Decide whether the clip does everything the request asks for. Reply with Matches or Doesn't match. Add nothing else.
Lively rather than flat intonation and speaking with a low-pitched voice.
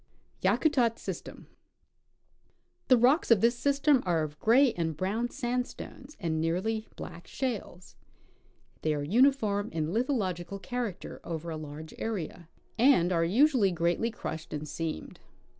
Doesn't match